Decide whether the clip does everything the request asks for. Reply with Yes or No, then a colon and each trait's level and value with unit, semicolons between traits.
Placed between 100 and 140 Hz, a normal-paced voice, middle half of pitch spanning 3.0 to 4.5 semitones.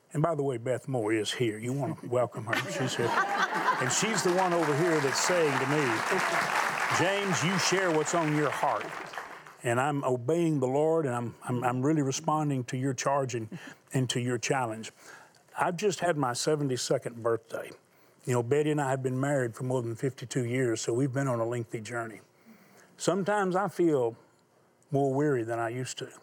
Yes: low, 135 Hz; average, 195 wpm; average, 4.1 semitones